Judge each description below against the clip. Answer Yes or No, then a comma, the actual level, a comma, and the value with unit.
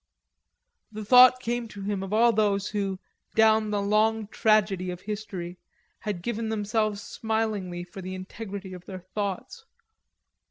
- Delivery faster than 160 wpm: No, average, 145 wpm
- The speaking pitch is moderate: No, high, 210 Hz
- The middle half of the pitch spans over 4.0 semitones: No, narrow, 2.4 semitones